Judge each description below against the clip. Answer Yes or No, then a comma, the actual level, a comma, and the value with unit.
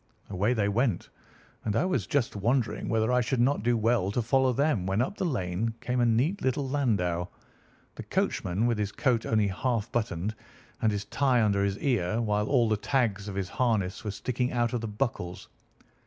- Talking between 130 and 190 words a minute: No, average, 200 wpm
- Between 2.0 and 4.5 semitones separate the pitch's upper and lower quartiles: Yes, average, 3.7 semitones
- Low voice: Yes, low, 115 Hz